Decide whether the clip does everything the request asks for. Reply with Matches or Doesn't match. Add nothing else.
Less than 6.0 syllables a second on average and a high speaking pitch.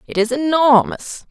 Matches